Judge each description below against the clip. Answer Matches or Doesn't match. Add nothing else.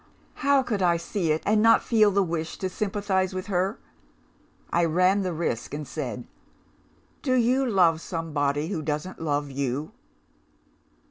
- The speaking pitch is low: Doesn't match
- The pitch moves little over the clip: Doesn't match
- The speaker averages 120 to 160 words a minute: Matches